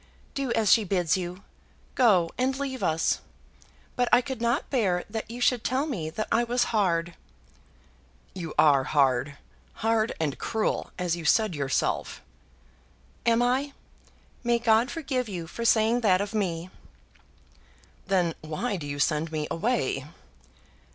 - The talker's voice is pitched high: Yes, high, 205 Hz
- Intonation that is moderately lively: No, wide, 6.5 semitones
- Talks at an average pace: Yes, average, 145 wpm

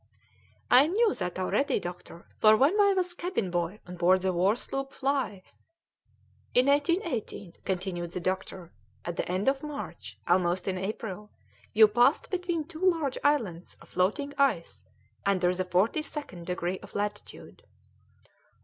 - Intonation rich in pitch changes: Yes, wide, 7.8 semitones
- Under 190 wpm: Yes, average, 150 wpm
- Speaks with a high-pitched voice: Yes, high, 210 Hz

